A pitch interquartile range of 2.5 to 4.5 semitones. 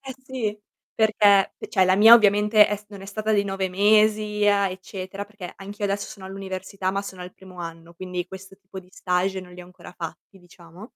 No: narrow, 2.0 semitones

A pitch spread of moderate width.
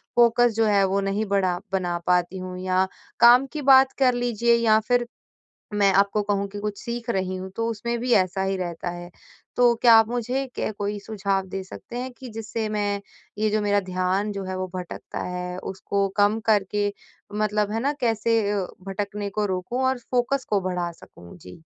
Yes: average, 3.6 semitones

